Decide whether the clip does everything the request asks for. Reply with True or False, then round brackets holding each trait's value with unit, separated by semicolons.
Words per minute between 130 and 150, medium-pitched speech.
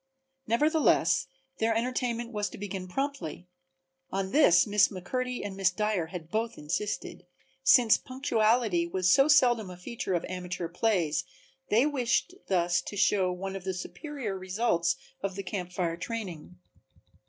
False (145 wpm; 200 Hz)